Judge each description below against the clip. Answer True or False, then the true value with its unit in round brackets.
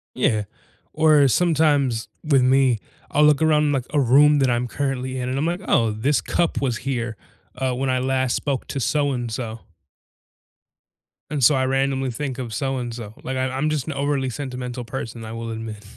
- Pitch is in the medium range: False (130 Hz)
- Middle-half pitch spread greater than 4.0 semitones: False (2.8 semitones)